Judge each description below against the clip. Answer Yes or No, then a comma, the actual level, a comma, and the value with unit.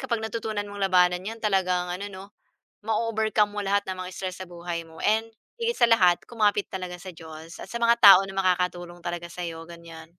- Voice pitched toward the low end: No, medium, 185 Hz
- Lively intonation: No, average, 3.3 semitones